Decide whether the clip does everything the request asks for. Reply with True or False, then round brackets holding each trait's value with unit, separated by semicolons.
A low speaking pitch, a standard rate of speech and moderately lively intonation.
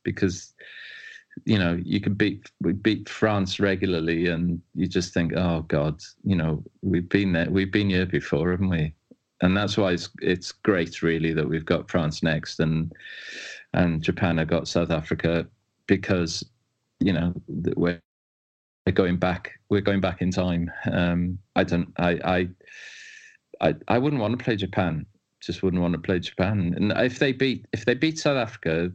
True (90 Hz; 175 wpm; 3.4 semitones)